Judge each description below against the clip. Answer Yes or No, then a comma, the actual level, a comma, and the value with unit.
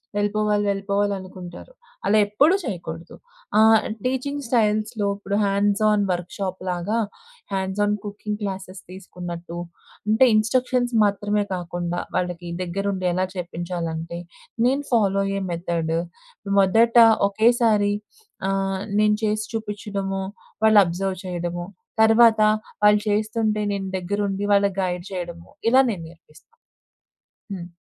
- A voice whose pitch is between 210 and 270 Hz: No, high, 200 Hz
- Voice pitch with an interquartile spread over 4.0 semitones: No, average, 3.0 semitones